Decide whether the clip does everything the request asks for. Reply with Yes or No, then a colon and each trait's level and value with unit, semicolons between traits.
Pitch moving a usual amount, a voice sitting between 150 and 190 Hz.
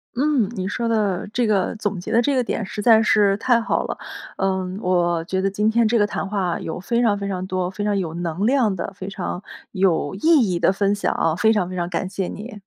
No: average, 3.1 semitones; high, 200 Hz